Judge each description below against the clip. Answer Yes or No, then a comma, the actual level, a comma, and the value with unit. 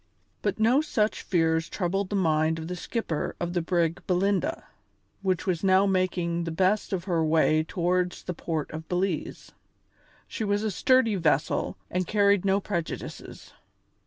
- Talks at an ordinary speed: Yes, average, 160 wpm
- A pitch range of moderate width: Yes, average, 3.3 semitones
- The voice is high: No, medium, 180 Hz